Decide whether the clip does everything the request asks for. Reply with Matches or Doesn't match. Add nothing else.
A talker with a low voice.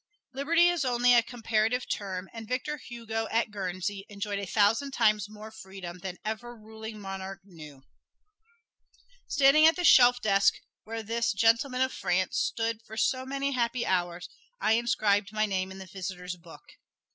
Doesn't match